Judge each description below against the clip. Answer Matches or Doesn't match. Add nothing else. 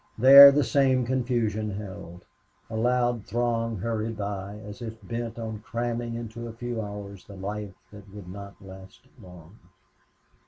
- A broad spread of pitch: Doesn't match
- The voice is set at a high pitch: Doesn't match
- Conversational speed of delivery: Matches